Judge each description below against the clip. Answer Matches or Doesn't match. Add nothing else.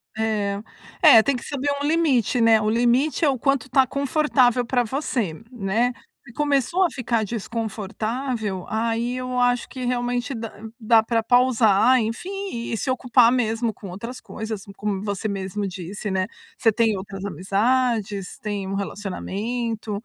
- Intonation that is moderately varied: Matches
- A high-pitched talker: Matches